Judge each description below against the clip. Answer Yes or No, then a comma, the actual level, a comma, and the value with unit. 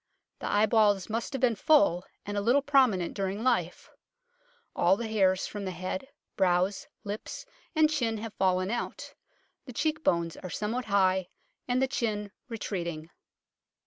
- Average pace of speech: Yes, average, 155 wpm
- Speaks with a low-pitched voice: No, high, 205 Hz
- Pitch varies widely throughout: No, average, 4.2 semitones